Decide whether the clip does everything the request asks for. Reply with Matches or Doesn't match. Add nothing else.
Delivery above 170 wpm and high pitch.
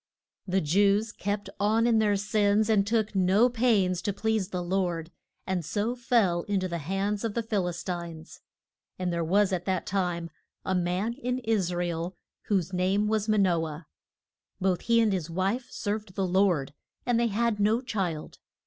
Matches